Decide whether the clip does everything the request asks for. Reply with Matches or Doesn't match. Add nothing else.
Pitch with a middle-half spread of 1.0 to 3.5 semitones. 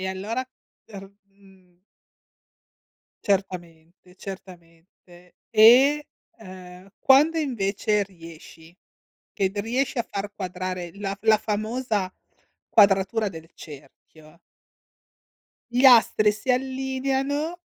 Doesn't match